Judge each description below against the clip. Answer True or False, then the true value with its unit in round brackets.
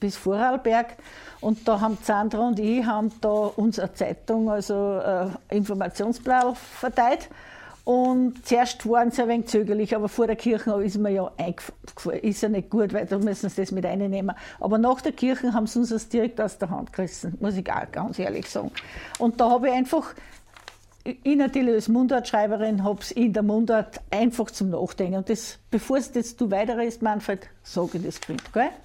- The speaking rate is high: True (195 wpm)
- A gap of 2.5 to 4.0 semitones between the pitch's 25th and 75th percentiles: True (2.9 semitones)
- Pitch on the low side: False (220 Hz)